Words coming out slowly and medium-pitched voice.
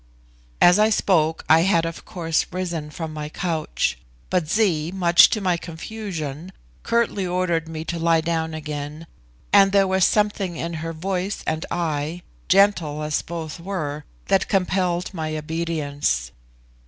No: average, 145 wpm; medium, 170 Hz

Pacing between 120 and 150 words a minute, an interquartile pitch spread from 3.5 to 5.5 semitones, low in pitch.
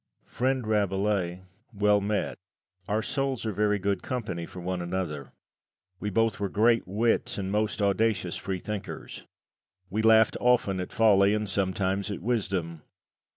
No: average, 140 wpm; average, 2.7 semitones; low, 100 Hz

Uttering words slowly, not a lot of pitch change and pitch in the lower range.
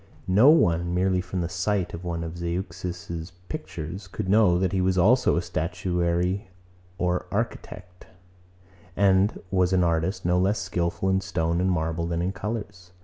No: average, 160 wpm; narrow, 1.8 semitones; very low, 90 Hz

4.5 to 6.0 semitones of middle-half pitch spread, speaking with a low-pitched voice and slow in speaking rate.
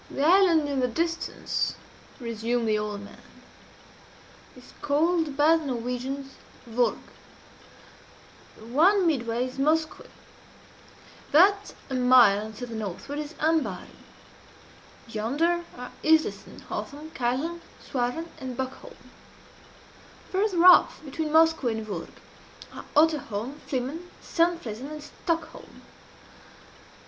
No: average, 5.1 semitones; very high, 280 Hz; slow, 105 wpm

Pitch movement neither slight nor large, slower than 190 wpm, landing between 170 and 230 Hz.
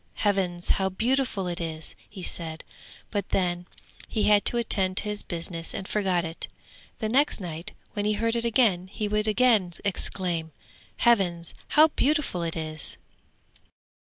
Yes: average, 3.9 semitones; average, 155 wpm; high, 190 Hz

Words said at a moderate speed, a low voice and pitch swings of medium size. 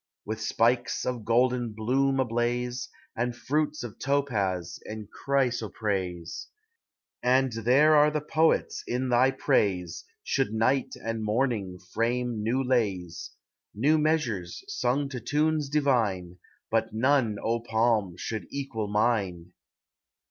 No: slow, 120 wpm; low, 120 Hz; average, 3.9 semitones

